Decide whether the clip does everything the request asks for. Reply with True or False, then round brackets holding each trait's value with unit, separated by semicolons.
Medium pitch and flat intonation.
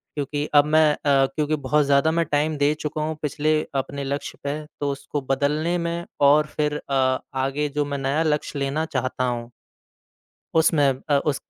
True (145 Hz; 1.7 semitones)